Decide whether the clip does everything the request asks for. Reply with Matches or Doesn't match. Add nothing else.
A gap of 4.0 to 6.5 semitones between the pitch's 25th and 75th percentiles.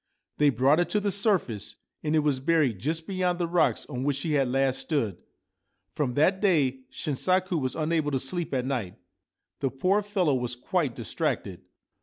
Matches